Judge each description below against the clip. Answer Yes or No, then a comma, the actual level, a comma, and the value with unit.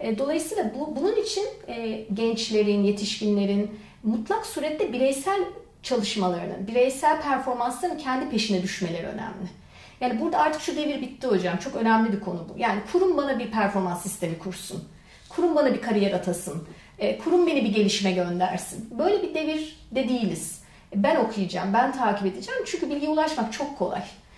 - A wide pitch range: Yes, wide, 7.4 semitones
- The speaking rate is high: Yes, fast, 155 wpm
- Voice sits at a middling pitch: No, high, 230 Hz